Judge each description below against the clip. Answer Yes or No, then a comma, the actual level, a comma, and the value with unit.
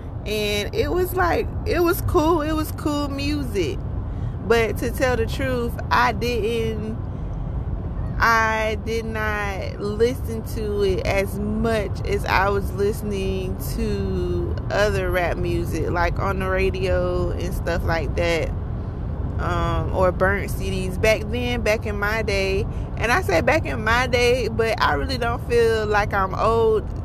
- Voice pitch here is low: Yes, low, 100 Hz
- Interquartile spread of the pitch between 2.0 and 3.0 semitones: No, average, 3.4 semitones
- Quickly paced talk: No, average, 150 wpm